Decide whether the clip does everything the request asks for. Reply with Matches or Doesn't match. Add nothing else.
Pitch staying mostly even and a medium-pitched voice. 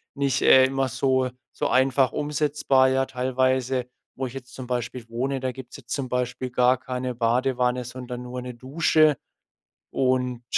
Doesn't match